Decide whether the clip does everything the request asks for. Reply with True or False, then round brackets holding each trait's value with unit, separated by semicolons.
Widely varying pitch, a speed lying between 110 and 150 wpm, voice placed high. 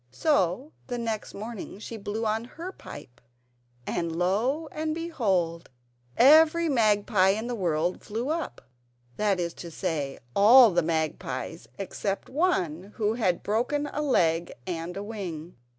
True (6.1 semitones; 140 wpm; 205 Hz)